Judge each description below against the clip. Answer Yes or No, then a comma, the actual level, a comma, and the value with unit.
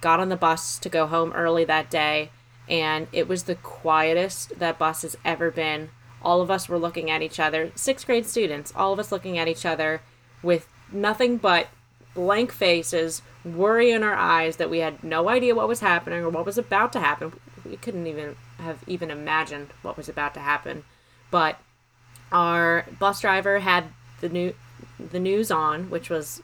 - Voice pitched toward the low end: No, medium, 165 Hz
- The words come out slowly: No, average, 190 wpm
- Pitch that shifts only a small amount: No, average, 3.0 semitones